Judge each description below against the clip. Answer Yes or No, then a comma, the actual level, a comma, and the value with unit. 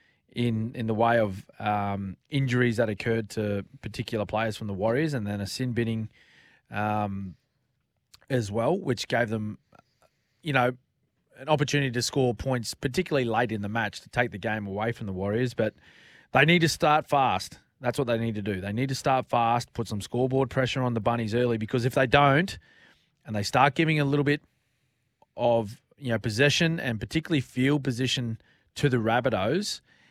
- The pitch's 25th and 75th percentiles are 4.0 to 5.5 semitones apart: No, average, 3.3 semitones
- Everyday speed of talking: Yes, average, 185 wpm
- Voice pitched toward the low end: Yes, low, 120 Hz